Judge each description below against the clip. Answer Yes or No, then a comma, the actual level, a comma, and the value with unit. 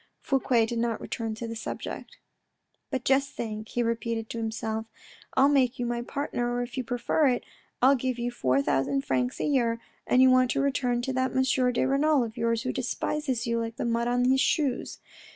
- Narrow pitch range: Yes, narrow, 2.2 semitones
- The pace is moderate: No, fast, 215 wpm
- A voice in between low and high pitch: No, high, 245 Hz